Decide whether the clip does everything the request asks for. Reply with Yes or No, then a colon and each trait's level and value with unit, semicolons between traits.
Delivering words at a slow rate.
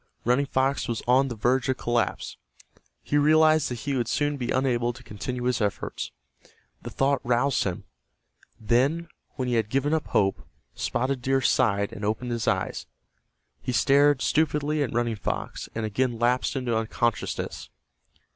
No: average, 160 wpm